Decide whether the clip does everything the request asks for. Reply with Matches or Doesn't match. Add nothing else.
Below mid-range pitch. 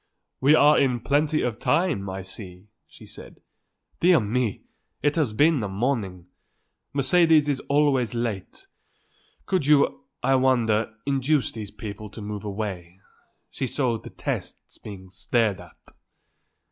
Matches